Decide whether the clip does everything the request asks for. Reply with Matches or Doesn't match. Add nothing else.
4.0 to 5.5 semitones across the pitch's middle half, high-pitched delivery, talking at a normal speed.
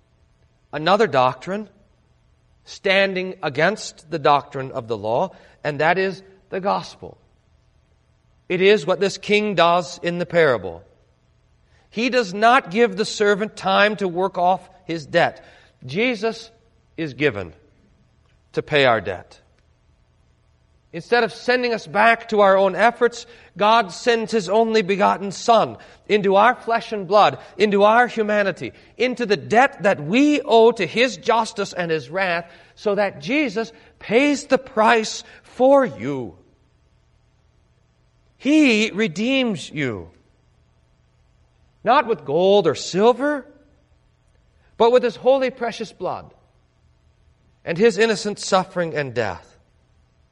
Doesn't match